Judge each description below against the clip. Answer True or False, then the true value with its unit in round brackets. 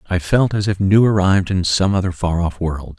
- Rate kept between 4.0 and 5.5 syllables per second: True (5.4 syllables/s)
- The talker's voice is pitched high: False (95 Hz)